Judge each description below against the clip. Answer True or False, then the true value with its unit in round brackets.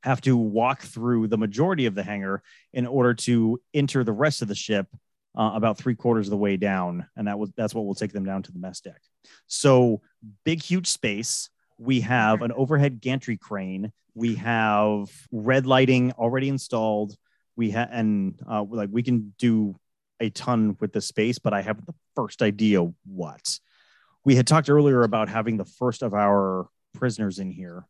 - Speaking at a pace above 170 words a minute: True (190 wpm)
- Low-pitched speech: True (115 Hz)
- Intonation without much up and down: False (3.3 semitones)